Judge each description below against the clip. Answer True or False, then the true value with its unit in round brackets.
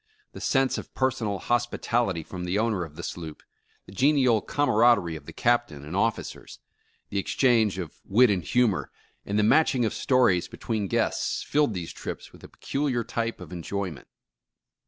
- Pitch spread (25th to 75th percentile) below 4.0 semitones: False (5.1 semitones)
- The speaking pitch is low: True (110 Hz)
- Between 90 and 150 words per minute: False (175 wpm)